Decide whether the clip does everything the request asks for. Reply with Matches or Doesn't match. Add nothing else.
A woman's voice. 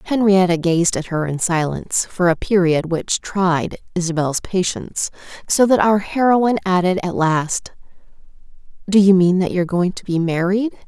Matches